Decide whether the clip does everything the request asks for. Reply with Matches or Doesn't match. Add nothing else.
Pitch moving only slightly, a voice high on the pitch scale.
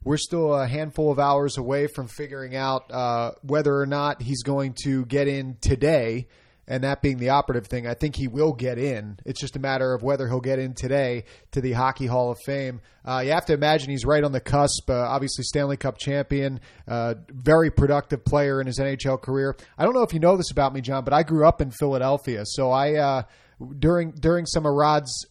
Doesn't match